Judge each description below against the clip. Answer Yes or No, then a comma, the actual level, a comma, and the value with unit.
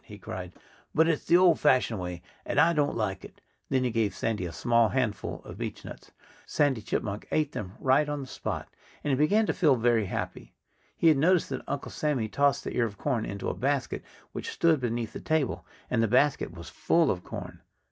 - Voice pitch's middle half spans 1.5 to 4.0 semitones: No, average, 5.3 semitones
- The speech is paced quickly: Yes, fast, 210 wpm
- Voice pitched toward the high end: No, low, 130 Hz